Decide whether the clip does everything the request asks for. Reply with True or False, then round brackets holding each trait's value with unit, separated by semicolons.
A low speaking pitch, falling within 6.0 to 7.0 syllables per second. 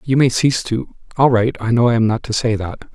False (120 Hz; 5.7 syllables/s)